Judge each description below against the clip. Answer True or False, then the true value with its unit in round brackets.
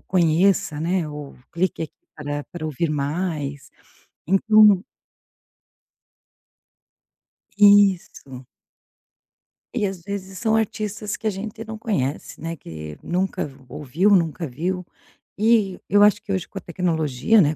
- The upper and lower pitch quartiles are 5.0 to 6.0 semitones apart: True (5.3 semitones)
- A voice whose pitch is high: False (180 Hz)